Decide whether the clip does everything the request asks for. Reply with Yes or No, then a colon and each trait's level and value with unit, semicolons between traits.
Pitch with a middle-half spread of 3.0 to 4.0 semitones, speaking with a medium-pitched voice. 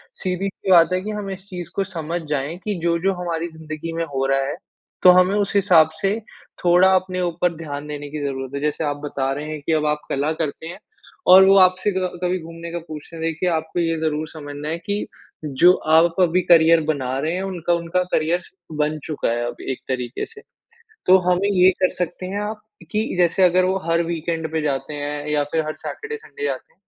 Yes: average, 3.4 semitones; medium, 165 Hz